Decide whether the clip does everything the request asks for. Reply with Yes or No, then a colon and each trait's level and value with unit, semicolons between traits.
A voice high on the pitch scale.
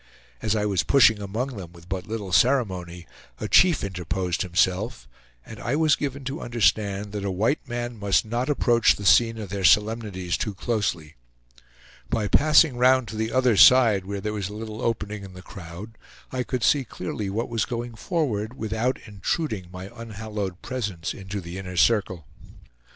No: low, 105 Hz